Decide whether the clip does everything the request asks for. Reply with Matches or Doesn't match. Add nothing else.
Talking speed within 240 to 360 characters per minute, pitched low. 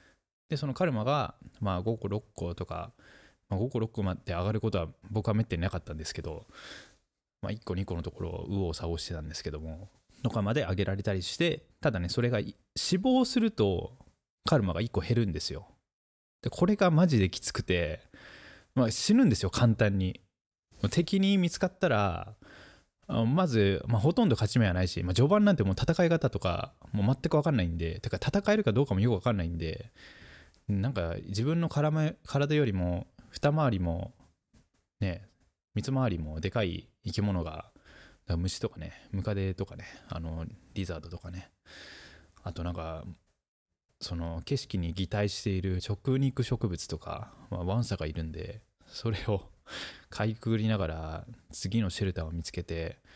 Matches